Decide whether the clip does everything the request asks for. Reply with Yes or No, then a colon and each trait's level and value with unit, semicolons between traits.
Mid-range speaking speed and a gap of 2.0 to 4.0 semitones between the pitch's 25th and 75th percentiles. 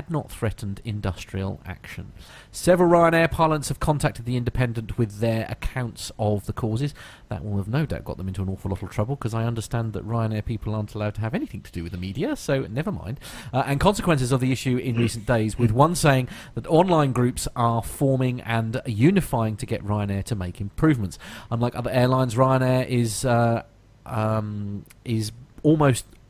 Yes: average, 190 wpm; average, 3.7 semitones